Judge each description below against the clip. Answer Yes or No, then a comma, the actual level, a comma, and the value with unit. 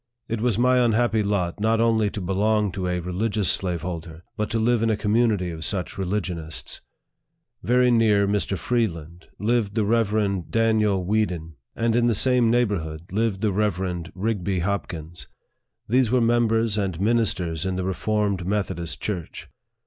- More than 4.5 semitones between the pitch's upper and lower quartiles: No, average, 3.9 semitones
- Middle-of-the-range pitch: No, low, 105 Hz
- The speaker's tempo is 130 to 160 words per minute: Yes, average, 155 wpm